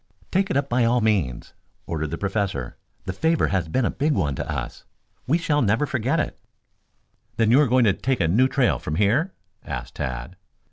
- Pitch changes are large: Yes, wide, 7.0 semitones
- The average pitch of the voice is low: Yes, low, 115 Hz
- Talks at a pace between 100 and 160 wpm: No, average, 200 wpm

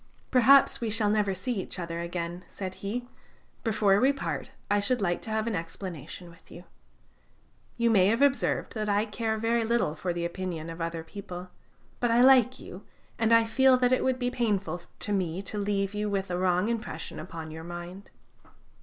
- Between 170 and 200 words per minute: Yes, average, 195 wpm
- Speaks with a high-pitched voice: Yes, high, 200 Hz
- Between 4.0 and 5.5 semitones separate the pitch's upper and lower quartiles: Yes, average, 4.6 semitones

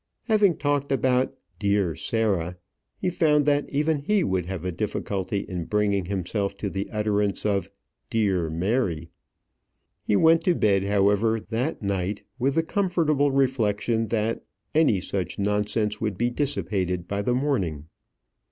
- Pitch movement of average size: No, wide, 5.9 semitones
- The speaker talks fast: No, average, 145 wpm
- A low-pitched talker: Yes, low, 105 Hz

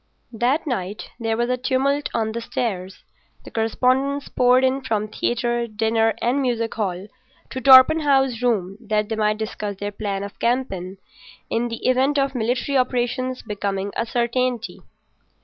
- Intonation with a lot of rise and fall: No, average, 3.2 semitones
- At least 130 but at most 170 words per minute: Yes, average, 150 wpm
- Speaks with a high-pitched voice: Yes, high, 235 Hz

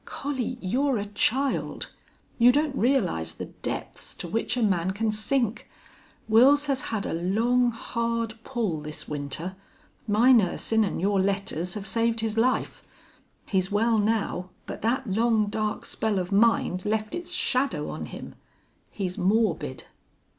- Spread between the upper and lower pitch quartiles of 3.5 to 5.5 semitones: Yes, average, 3.8 semitones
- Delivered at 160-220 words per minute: No, average, 145 wpm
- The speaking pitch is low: No, high, 220 Hz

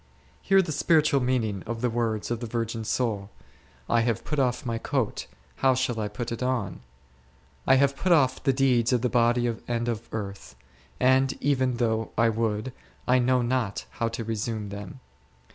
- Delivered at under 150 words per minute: No, average, 185 wpm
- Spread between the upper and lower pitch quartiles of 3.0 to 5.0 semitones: No, narrow, 2.5 semitones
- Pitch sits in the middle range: No, low, 120 Hz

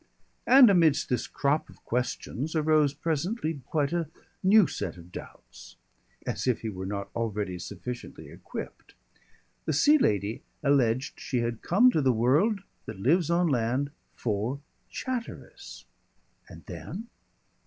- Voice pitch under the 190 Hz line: Yes, medium, 140 Hz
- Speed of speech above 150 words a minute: No, slow, 135 wpm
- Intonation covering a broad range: Yes, wide, 6.6 semitones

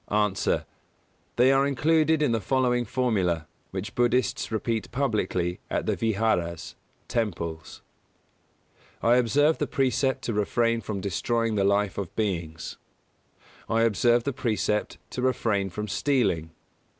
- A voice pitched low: Yes, low, 115 Hz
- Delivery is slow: Yes, slow, 130 wpm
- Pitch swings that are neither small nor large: Yes, average, 4.3 semitones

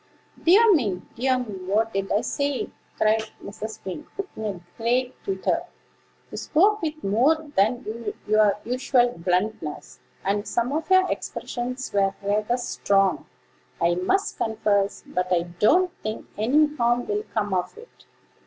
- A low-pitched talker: No, high, 225 Hz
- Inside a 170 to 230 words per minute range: No, average, 145 wpm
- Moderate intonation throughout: No, wide, 5.8 semitones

